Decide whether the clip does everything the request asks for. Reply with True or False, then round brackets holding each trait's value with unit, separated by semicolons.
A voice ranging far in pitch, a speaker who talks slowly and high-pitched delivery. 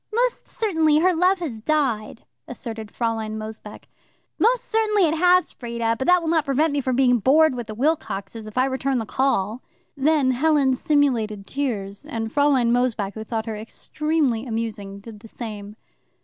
False (5.7 semitones; 170 wpm; 255 Hz)